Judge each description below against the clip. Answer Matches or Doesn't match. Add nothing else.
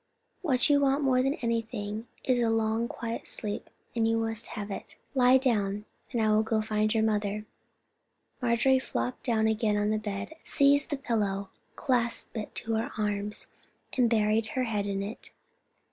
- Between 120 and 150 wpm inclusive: Doesn't match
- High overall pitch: Matches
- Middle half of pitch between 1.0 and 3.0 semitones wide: Matches